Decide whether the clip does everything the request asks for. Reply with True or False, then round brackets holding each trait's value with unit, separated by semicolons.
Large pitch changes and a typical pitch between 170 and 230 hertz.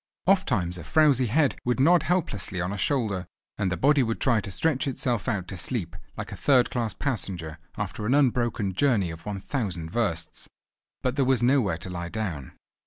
False (6.6 semitones; 110 Hz)